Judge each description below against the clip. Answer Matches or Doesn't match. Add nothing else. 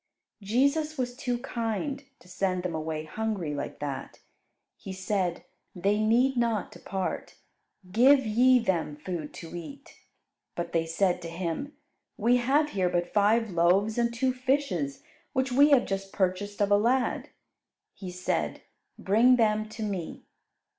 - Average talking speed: Matches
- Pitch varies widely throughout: Matches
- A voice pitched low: Doesn't match